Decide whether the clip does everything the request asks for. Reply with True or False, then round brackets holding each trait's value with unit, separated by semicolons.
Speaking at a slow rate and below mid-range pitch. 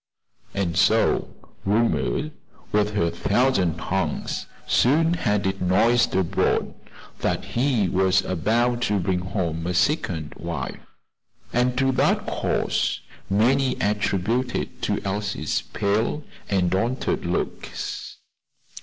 True (105 wpm; 105 Hz)